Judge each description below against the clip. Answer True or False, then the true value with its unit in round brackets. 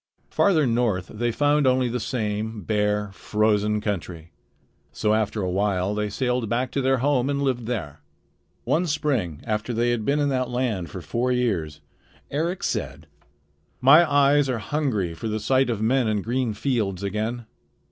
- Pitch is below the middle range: True (115 Hz)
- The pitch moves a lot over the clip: False (4.0 semitones)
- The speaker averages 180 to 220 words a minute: False (165 wpm)